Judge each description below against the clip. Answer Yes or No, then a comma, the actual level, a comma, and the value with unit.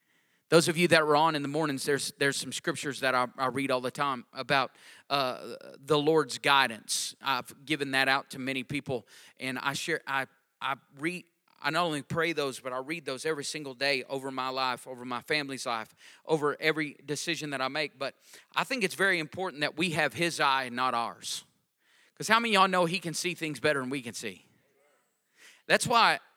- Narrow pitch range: No, average, 3.3 semitones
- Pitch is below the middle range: No, medium, 145 Hz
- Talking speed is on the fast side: Yes, fast, 215 wpm